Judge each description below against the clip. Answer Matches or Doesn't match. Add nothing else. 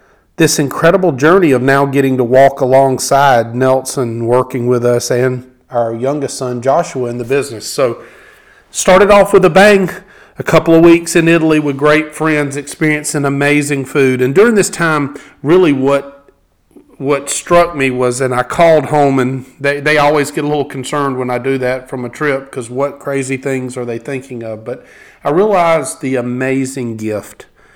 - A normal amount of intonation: Matches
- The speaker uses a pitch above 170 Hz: Doesn't match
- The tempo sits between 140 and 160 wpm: Doesn't match